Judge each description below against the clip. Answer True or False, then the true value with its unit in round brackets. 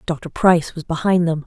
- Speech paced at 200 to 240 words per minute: True (205 wpm)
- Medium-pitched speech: True (165 Hz)